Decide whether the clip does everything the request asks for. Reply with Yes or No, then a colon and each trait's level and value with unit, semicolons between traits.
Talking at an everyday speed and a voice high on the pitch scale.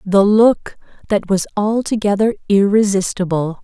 No: slow, 100 wpm; high, 205 Hz